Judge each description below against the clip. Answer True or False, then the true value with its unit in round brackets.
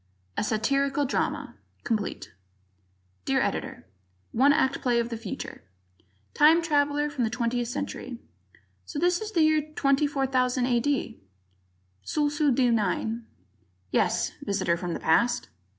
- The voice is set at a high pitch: True (260 Hz)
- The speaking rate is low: True (125 wpm)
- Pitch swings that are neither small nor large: True (3.9 semitones)